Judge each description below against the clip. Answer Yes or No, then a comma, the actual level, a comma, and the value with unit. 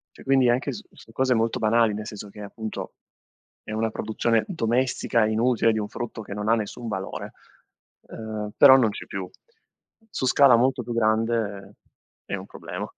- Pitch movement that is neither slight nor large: No, narrow, 2.1 semitones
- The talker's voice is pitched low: Yes, low, 115 Hz